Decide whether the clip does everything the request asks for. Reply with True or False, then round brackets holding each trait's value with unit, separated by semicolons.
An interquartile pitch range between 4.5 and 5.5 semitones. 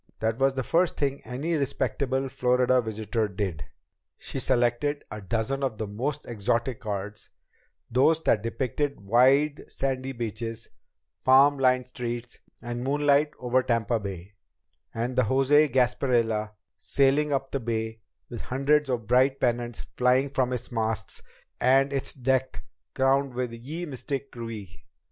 False (2.9 semitones)